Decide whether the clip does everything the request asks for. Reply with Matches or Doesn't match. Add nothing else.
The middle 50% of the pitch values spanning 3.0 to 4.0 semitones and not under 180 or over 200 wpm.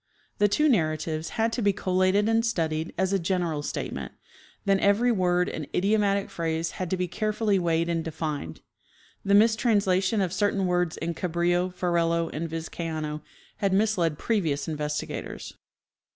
Doesn't match